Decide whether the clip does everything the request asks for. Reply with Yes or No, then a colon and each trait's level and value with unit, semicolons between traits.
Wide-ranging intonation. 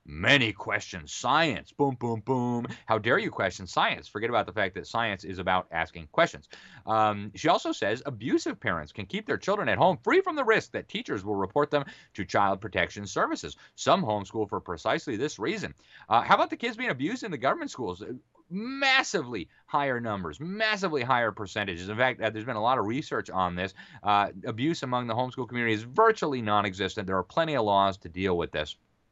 Yes: wide, 6.8 semitones